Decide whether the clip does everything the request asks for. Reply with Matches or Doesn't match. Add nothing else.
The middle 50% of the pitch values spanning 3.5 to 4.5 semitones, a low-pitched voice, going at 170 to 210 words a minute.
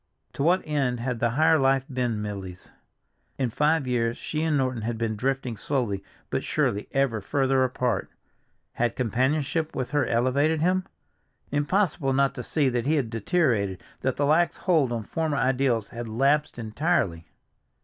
Doesn't match